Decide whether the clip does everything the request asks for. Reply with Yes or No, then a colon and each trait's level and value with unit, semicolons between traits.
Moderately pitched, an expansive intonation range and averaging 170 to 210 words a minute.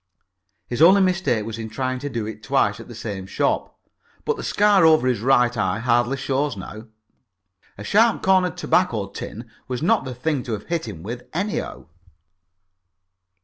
No: low, 125 Hz; wide, 7.1 semitones; average, 175 wpm